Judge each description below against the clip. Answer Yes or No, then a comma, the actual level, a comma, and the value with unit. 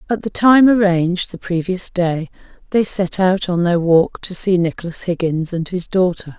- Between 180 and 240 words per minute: Yes, average, 190 wpm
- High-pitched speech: No, medium, 180 Hz